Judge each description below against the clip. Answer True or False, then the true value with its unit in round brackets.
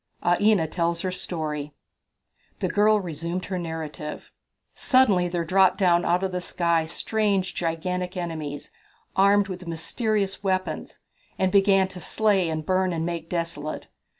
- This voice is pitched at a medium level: True (180 Hz)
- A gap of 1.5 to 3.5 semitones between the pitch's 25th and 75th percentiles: True (2.7 semitones)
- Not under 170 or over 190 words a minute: False (140 wpm)